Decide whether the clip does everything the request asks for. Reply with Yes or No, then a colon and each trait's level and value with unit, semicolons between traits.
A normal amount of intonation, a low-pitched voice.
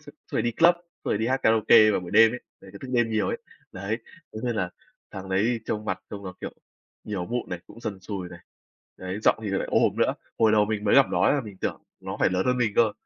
Yes: average, 3.4 semitones; low, 105 Hz